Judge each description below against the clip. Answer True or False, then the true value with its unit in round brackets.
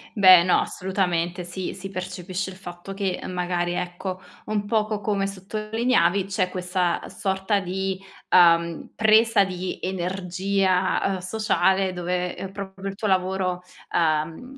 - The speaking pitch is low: False (185 Hz)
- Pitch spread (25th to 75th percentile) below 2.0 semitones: True (1.6 semitones)